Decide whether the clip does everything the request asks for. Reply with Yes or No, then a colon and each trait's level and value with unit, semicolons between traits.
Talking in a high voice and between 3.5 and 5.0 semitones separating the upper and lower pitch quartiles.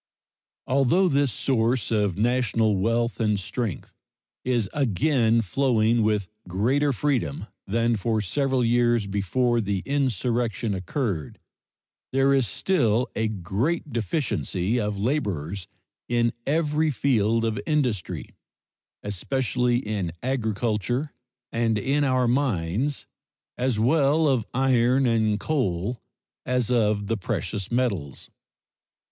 No: low, 115 Hz; average, 4.2 semitones